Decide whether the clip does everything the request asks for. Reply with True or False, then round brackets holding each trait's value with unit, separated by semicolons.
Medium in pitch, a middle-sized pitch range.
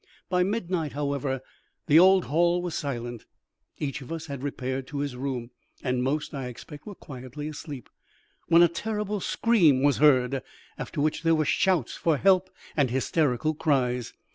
True (145 Hz; 4.4 semitones)